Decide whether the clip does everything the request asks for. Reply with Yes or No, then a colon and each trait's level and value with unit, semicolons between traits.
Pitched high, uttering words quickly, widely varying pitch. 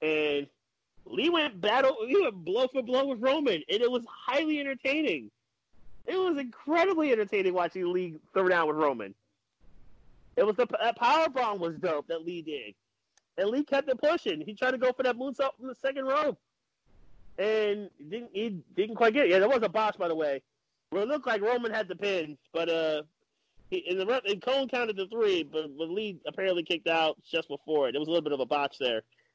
Yes: high, 210 Hz; fast, 215 wpm; wide, 8.7 semitones